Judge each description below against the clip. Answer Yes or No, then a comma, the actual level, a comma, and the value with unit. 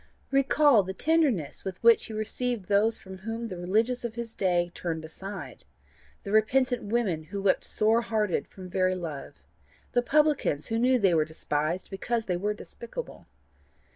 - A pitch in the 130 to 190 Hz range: No, high, 210 Hz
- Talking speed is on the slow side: No, average, 165 wpm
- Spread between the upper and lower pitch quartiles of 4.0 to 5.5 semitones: Yes, average, 4.5 semitones